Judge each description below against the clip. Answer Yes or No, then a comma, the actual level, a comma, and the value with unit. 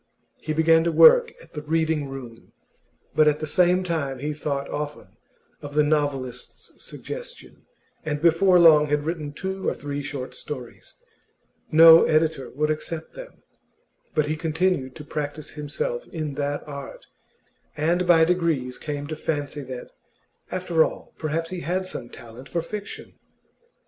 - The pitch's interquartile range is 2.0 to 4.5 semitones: Yes, narrow, 2.6 semitones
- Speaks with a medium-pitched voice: Yes, medium, 155 Hz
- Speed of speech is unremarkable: Yes, average, 150 wpm